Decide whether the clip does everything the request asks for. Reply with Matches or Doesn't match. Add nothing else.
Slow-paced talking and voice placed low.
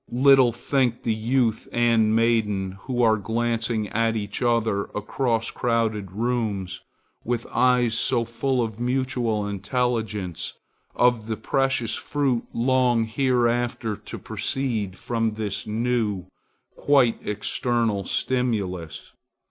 Matches